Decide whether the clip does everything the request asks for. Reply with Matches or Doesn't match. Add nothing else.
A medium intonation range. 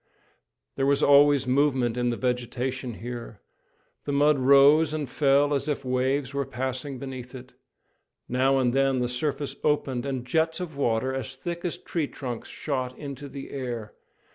Doesn't match